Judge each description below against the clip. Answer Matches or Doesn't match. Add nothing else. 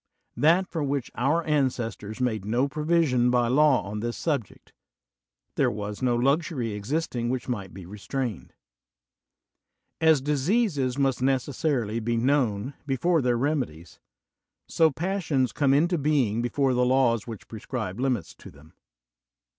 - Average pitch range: Matches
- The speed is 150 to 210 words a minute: Doesn't match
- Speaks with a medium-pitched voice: Doesn't match